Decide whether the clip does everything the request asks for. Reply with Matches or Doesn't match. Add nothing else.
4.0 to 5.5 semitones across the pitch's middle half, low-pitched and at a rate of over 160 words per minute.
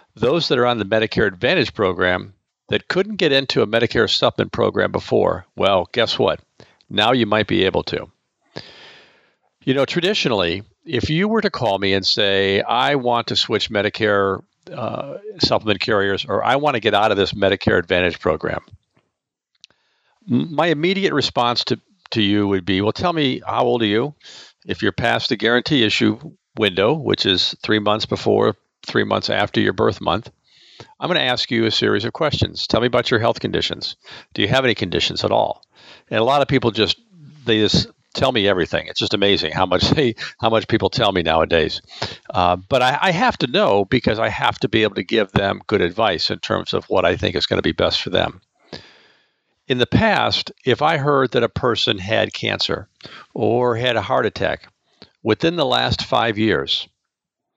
Matches